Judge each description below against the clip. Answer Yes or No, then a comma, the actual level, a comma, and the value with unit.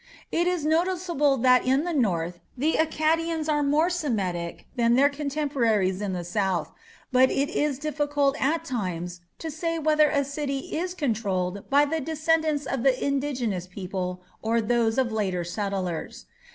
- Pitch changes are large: Yes, wide, 7.1 semitones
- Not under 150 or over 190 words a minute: Yes, average, 155 wpm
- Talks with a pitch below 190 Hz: No, very high, 270 Hz